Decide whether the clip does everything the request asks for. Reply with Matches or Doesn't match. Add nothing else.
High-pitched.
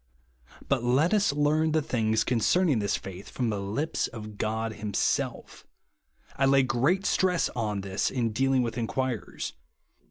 Doesn't match